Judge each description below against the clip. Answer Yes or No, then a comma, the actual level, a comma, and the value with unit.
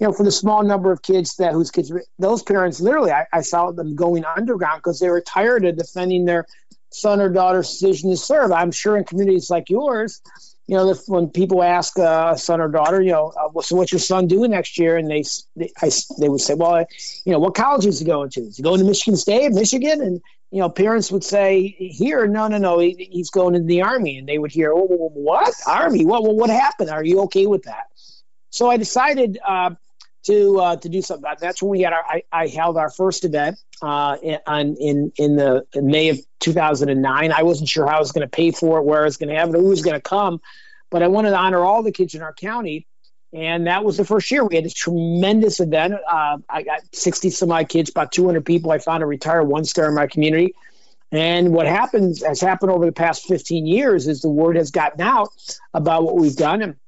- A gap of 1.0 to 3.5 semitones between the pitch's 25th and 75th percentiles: Yes, average, 3.1 semitones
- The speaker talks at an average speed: No, fast, 245 wpm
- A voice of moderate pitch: Yes, medium, 175 Hz